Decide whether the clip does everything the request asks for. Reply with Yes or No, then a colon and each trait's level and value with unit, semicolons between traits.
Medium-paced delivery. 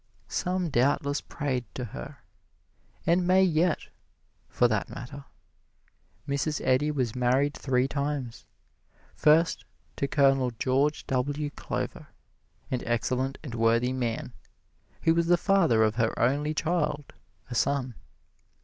No: slow, 120 wpm